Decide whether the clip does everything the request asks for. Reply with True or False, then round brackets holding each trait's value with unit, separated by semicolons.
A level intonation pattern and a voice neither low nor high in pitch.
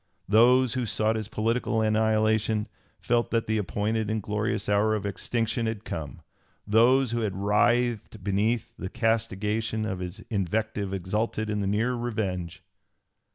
False (1.8 semitones; 110 Hz)